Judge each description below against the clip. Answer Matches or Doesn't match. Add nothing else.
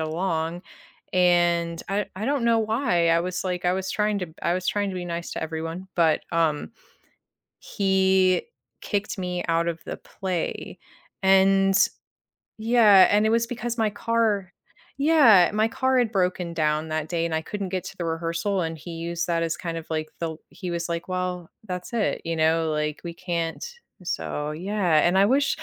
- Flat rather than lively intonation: Doesn't match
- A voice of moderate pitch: Matches